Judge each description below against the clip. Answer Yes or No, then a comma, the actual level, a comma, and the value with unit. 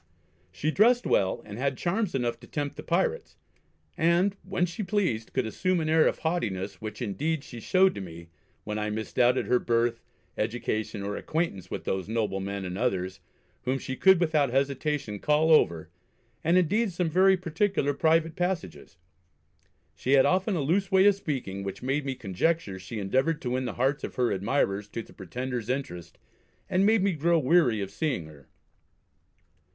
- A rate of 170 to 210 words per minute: Yes, average, 175 wpm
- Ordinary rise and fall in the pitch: No, wide, 8.1 semitones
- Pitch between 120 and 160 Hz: Yes, low, 135 Hz